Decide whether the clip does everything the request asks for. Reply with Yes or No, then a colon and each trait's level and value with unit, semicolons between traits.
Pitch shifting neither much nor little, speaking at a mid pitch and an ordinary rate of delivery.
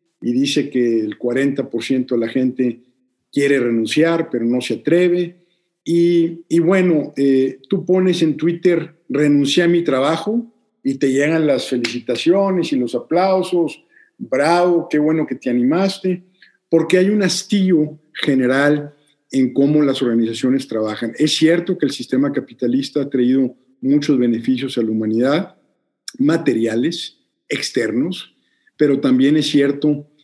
Yes: average, 5.0 semitones; medium, 145 Hz; average, 135 wpm